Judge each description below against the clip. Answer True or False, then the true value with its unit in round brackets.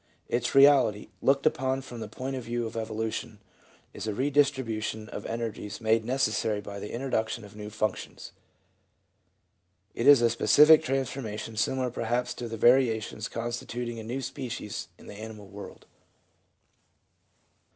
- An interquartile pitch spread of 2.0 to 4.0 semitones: True (3.3 semitones)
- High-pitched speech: False (115 Hz)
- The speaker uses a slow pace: False (145 wpm)